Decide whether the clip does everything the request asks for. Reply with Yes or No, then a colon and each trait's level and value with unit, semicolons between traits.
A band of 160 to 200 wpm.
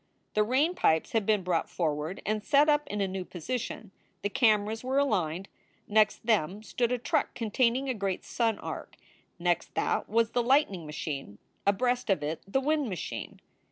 Yes: average, 180 wpm